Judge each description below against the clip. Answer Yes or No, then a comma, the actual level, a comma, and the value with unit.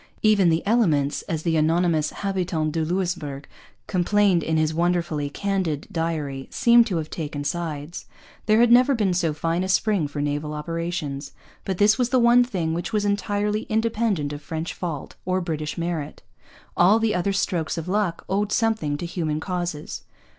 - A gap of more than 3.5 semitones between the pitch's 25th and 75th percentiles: Yes, average, 4.7 semitones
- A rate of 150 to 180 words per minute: Yes, average, 170 wpm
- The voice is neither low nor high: Yes, medium, 175 Hz